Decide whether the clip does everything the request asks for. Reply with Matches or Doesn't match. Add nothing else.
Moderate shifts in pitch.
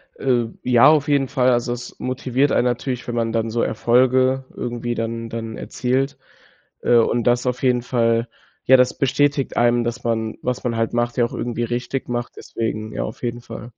Doesn't match